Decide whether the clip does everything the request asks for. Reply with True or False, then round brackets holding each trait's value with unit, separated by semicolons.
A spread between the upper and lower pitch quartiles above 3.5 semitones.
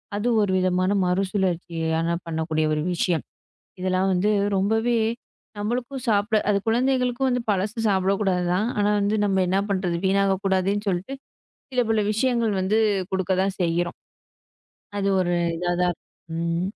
False (2.9 semitones)